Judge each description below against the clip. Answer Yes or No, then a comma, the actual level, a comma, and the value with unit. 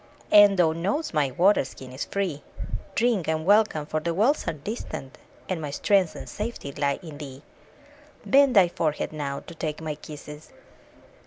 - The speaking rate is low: No, average, 170 wpm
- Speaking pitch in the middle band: Yes, medium, 160 Hz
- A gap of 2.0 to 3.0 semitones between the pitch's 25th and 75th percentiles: No, average, 5.3 semitones